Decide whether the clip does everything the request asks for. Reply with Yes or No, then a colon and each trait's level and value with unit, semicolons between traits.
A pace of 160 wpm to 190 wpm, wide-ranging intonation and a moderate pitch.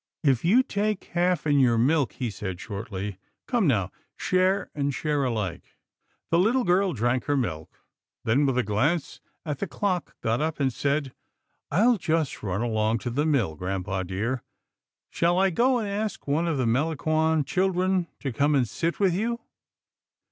Yes: average, 175 wpm; wide, 7.6 semitones; medium, 145 Hz